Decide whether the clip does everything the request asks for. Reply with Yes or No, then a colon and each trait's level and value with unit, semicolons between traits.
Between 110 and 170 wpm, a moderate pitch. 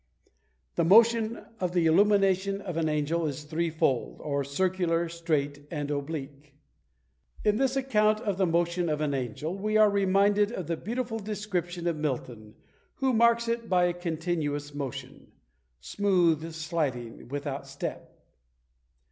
Yes: average, 140 wpm; medium, 170 Hz